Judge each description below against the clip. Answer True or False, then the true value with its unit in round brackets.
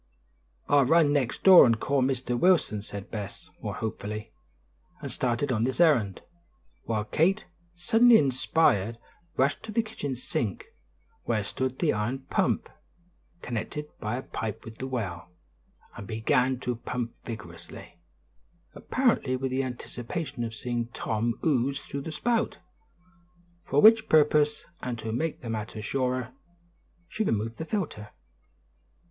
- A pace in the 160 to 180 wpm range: False (140 wpm)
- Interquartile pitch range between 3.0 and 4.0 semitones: False (5.0 semitones)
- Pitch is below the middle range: True (125 Hz)